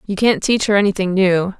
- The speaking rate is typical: No, fast, 225 wpm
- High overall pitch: Yes, high, 195 Hz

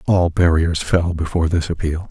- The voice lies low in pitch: Yes, very low, 85 Hz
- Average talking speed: Yes, average, 170 wpm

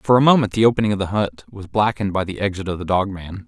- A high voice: No, low, 100 Hz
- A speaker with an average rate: No, fast, 295 wpm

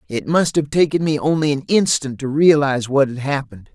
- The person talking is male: Yes, male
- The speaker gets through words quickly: Yes, fast, 210 wpm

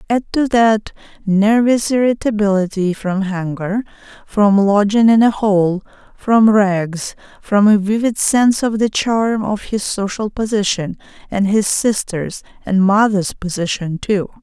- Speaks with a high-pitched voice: Yes, high, 205 Hz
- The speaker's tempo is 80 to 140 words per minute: Yes, slow, 135 wpm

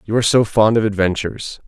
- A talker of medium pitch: No, low, 105 Hz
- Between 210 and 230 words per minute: Yes, fast, 215 wpm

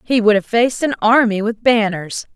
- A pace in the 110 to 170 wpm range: No, fast, 205 wpm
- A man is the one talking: No, female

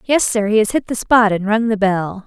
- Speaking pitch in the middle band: No, high, 215 Hz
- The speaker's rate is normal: No, fast, 290 wpm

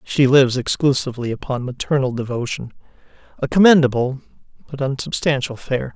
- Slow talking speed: Yes, slow, 110 wpm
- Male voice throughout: Yes, male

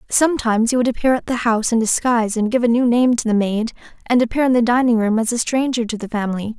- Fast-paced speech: Yes, fast, 265 wpm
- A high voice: Yes, high, 235 Hz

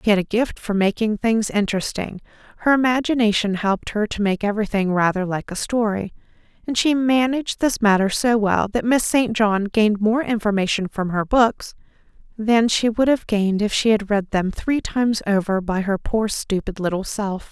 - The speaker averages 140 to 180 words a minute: No, average, 190 wpm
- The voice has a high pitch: Yes, high, 215 Hz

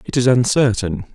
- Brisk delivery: No, average, 155 wpm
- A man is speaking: Yes, male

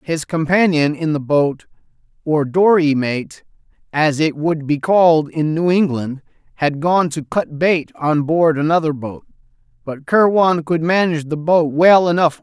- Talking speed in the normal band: Yes, average, 155 wpm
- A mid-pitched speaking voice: Yes, medium, 160 Hz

